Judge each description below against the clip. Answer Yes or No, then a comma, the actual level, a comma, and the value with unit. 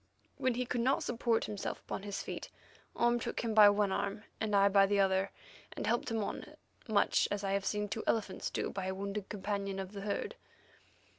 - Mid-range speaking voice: No, high, 205 Hz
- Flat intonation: Yes, narrow, 2.0 semitones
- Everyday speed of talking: No, fast, 210 wpm